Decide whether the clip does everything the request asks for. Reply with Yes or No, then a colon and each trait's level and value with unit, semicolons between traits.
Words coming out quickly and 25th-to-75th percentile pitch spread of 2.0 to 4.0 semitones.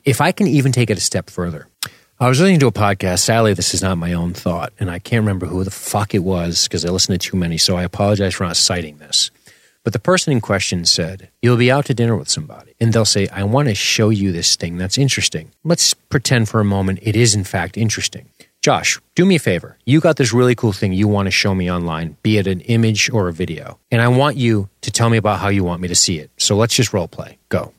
No: fast, 270 wpm; average, 4.6 semitones